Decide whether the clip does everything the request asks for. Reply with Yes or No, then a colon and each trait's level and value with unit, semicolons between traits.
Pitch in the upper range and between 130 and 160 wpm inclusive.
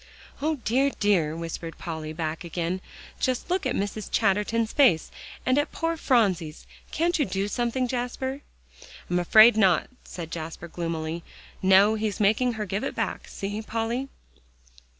Yes: high, 205 Hz; average, 150 wpm